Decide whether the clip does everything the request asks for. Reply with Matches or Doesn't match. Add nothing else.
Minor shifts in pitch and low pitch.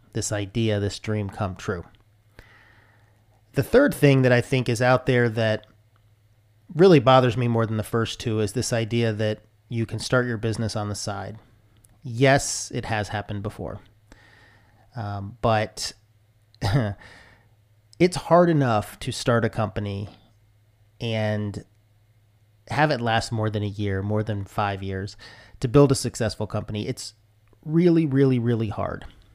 Matches